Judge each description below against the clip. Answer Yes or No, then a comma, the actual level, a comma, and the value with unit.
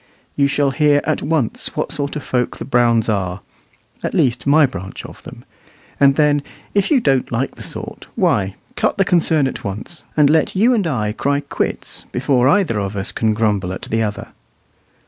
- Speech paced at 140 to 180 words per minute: No, average, 190 wpm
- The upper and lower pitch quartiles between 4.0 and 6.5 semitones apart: Yes, wide, 5.4 semitones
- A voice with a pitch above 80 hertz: Yes, low, 135 Hz